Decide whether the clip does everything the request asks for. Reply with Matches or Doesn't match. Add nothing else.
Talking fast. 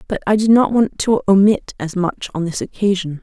Matches